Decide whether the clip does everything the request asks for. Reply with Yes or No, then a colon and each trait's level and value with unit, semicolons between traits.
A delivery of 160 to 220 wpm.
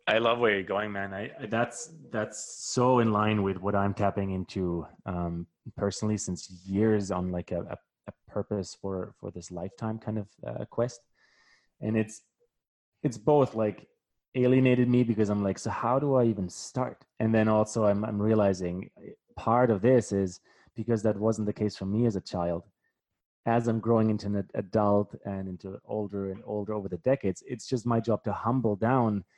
Yes: average, 185 wpm